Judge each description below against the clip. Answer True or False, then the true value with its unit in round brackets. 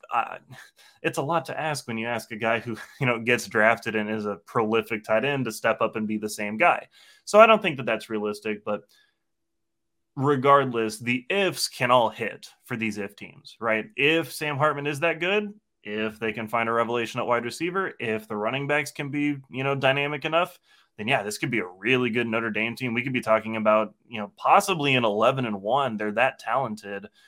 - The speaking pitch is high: False (120 Hz)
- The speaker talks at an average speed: False (220 wpm)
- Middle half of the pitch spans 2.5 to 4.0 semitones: False (5.1 semitones)